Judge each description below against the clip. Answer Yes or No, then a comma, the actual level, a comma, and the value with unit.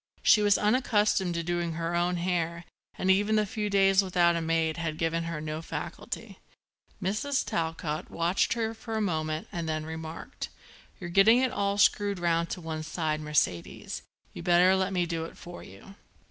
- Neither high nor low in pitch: Yes, medium, 175 Hz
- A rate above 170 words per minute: Yes, average, 180 wpm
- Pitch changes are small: No, average, 3.4 semitones